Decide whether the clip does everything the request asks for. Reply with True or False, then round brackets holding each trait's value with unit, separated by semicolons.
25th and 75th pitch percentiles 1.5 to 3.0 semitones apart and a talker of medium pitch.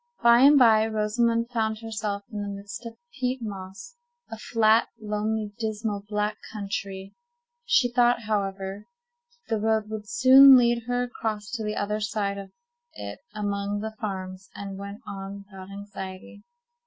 False (2.6 semitones; 215 Hz)